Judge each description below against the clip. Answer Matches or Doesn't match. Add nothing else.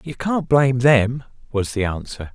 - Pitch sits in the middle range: Doesn't match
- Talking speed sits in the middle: Matches